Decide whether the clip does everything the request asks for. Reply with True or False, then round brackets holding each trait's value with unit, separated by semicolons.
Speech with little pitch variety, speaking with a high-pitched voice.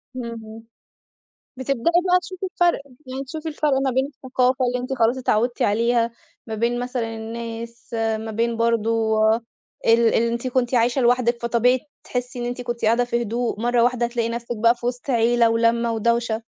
True (1.4 semitones; 235 Hz)